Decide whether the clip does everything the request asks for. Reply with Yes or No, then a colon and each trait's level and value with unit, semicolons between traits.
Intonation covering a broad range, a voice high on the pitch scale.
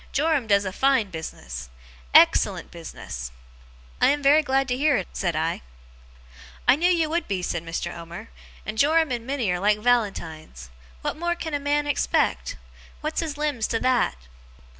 Yes: wide, 8.3 semitones; high, 245 Hz